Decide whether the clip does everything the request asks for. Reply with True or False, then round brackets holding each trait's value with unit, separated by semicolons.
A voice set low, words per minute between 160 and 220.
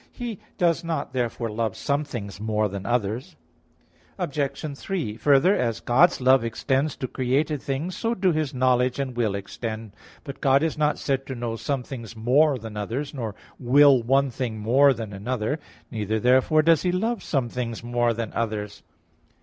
True (130 Hz; 175 wpm)